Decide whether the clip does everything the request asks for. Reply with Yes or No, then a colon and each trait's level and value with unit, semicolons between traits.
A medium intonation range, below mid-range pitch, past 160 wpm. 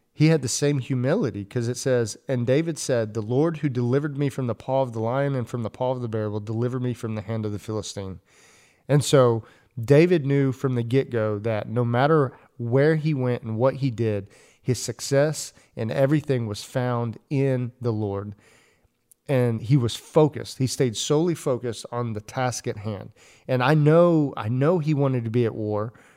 Yes: average, 3.5 semitones; low, 125 Hz; average, 200 wpm